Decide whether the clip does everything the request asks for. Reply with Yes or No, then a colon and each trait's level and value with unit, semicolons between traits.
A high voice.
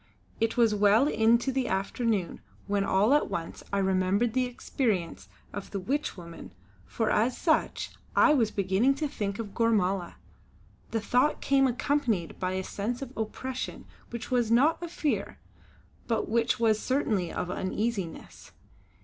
Yes: high, 225 Hz